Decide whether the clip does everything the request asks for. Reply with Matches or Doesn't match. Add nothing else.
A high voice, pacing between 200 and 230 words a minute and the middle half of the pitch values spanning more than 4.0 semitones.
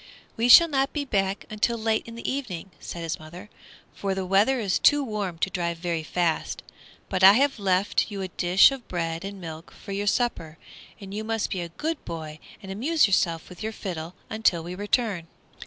Matches